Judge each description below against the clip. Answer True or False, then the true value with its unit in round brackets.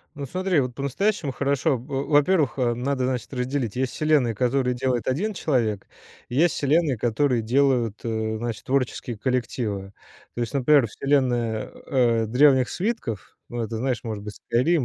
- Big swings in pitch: False (3.3 semitones)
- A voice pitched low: True (130 Hz)